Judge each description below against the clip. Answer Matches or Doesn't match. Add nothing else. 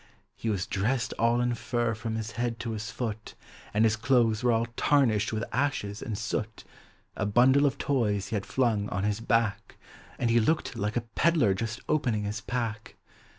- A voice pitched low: Matches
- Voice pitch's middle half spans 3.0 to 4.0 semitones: Doesn't match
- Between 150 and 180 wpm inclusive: Doesn't match